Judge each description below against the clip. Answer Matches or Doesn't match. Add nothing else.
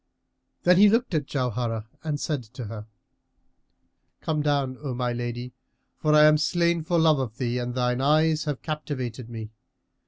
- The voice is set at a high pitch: Doesn't match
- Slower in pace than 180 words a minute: Matches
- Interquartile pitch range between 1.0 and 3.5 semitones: Doesn't match